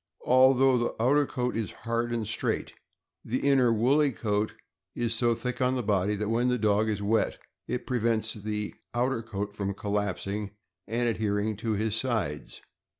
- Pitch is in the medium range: No, low, 115 Hz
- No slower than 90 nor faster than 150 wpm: No, average, 165 wpm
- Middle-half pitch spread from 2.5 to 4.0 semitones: Yes, average, 2.9 semitones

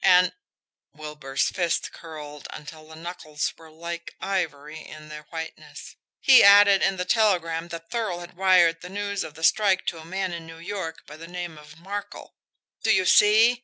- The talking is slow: No, average, 180 wpm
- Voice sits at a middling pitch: Yes, medium, 170 Hz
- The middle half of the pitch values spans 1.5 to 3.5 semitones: Yes, average, 3.2 semitones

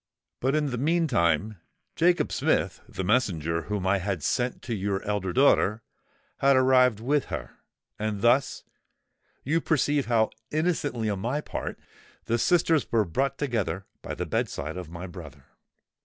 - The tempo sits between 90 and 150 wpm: Yes, average, 140 wpm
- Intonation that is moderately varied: No, wide, 6.6 semitones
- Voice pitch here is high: No, low, 115 Hz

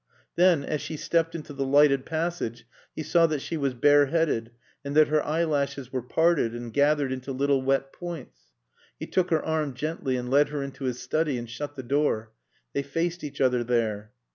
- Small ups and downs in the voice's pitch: No, average, 3.3 semitones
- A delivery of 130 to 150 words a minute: No, average, 190 wpm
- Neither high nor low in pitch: Yes, medium, 145 Hz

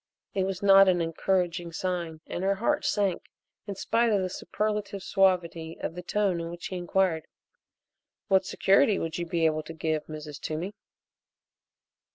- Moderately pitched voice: Yes, medium, 180 Hz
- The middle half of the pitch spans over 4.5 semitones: No, average, 2.9 semitones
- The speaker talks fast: No, average, 165 wpm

